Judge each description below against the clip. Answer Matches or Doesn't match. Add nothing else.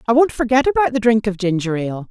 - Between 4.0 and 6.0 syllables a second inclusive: Doesn't match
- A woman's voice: Matches